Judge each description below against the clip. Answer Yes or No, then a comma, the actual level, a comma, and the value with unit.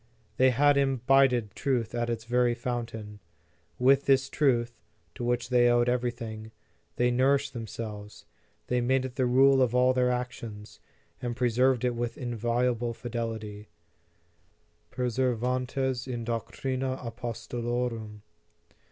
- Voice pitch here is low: Yes, low, 120 Hz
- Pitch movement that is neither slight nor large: No, narrow, 1.7 semitones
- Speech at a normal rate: No, slow, 120 wpm